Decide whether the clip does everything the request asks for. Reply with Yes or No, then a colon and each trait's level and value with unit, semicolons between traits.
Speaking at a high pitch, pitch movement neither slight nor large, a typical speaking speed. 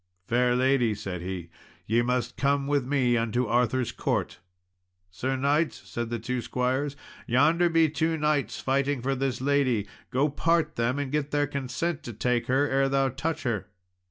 No: low, 130 Hz; average, 3.0 semitones; average, 170 wpm